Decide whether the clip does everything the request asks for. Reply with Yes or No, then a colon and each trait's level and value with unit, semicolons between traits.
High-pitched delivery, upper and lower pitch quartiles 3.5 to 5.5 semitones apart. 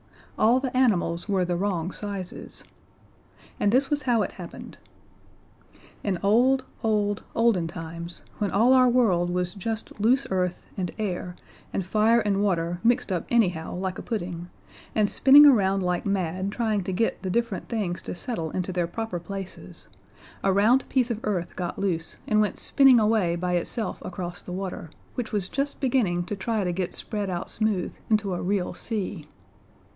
Yes: high, 200 Hz; average, 4.0 semitones